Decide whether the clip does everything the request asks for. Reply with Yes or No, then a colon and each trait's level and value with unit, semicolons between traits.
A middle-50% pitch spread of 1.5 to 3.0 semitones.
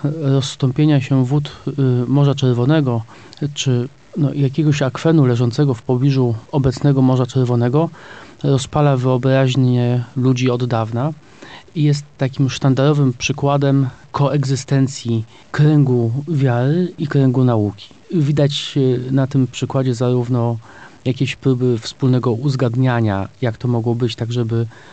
Yes: narrow, 2.5 semitones